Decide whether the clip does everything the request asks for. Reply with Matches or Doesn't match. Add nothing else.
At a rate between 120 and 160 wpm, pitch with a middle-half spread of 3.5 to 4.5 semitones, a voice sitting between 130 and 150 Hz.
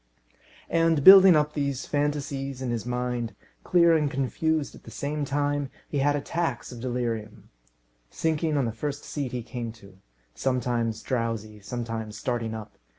Matches